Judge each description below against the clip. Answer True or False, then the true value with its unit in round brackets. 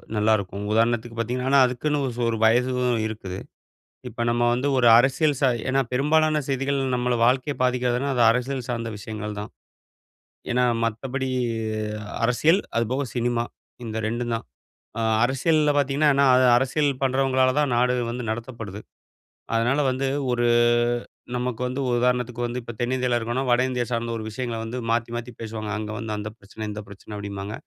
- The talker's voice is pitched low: True (125 Hz)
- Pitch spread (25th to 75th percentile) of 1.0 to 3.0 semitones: True (2.5 semitones)